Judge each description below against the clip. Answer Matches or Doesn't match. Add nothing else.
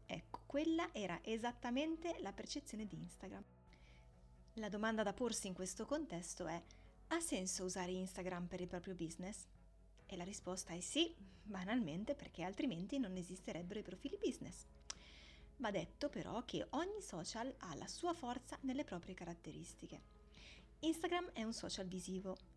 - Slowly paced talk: Doesn't match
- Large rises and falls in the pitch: Matches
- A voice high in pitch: Matches